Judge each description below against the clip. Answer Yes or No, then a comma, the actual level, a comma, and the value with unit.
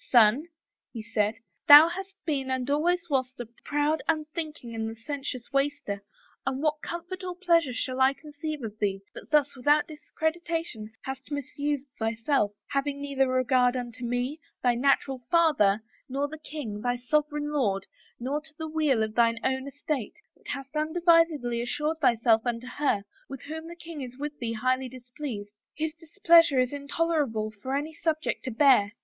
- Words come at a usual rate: Yes, average, 170 wpm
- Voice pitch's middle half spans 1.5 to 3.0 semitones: No, average, 4.0 semitones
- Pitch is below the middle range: No, very high, 275 Hz